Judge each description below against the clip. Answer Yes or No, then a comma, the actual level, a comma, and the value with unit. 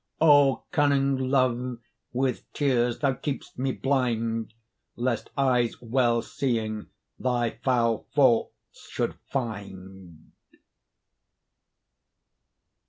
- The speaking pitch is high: No, low, 125 Hz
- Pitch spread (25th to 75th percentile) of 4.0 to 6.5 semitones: No, average, 2.8 semitones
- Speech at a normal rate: No, slow, 85 wpm